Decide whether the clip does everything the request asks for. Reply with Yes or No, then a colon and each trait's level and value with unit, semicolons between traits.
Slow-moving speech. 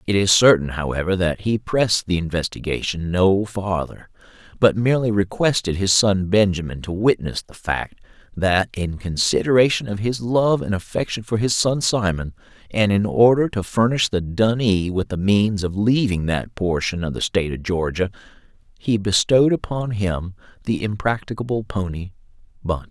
No: average, 155 wpm